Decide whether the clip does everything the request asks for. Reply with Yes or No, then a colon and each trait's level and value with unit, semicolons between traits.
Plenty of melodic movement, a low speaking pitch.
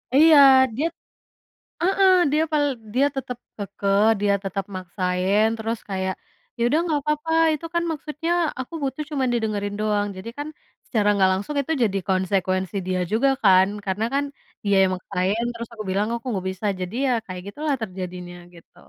No: wide, 6.6 semitones; high, 210 Hz